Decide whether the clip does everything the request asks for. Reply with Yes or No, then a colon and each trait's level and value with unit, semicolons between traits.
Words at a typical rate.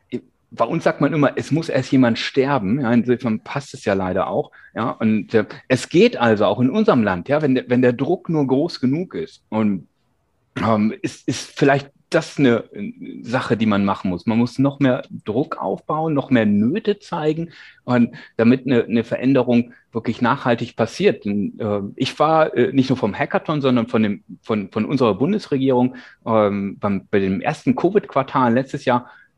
Yes: average, 180 wpm